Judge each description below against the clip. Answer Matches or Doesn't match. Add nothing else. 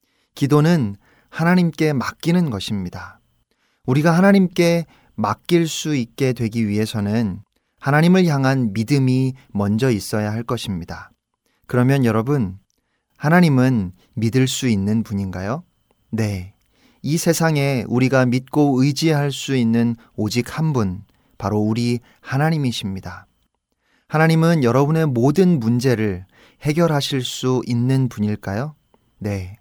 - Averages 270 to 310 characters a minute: Doesn't match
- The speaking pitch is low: Matches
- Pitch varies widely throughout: Matches